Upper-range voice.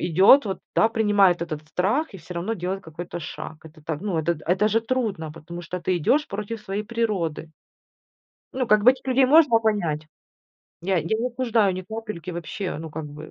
Yes: high, 195 Hz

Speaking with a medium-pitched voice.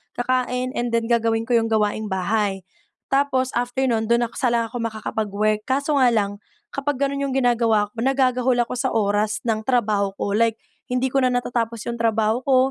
No: high, 235 Hz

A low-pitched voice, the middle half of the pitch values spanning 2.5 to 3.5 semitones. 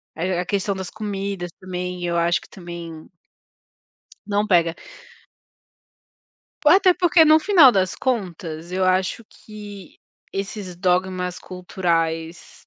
No: medium, 185 Hz; average, 2.9 semitones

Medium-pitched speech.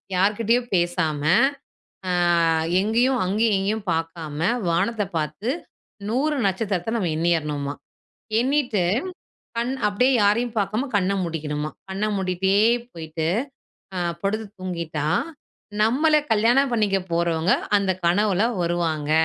No: high, 195 Hz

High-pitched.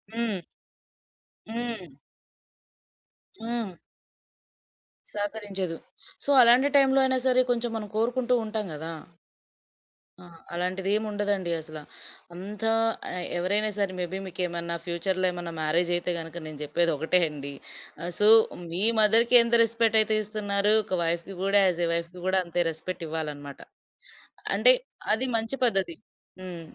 Yes: high, 195 Hz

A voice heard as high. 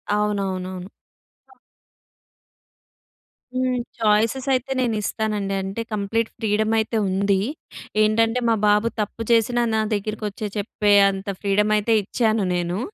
Yes: high, 210 Hz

